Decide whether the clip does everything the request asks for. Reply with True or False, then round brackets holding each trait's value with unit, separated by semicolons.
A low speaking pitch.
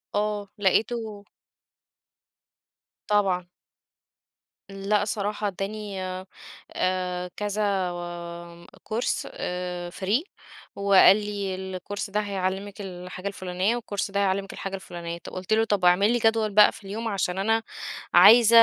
False (200 Hz)